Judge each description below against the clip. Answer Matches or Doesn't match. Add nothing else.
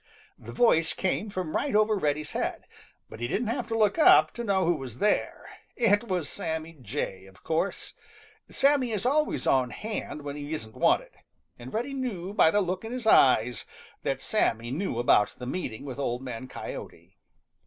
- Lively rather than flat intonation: Matches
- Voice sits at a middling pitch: Matches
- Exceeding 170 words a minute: Matches